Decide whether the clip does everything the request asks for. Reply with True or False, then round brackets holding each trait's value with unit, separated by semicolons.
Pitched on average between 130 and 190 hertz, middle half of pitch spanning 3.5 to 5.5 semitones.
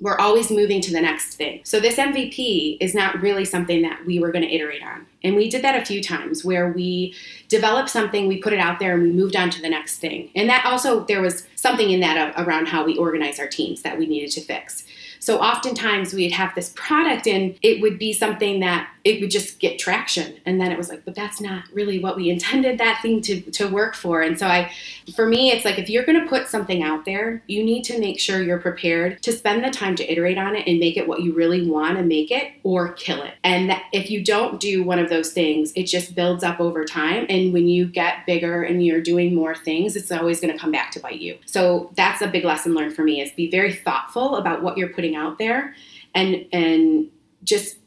True (185 Hz; 3.8 semitones)